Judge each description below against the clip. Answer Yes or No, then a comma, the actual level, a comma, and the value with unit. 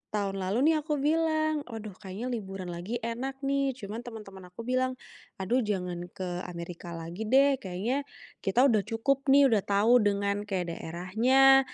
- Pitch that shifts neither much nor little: No, wide, 5.8 semitones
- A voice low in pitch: No, high, 220 Hz